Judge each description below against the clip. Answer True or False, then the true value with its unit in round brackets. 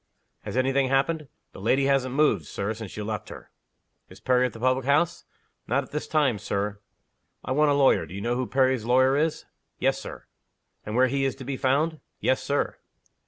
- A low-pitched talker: True (130 Hz)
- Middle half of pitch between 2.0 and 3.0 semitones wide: True (2.4 semitones)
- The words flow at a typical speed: False (210 wpm)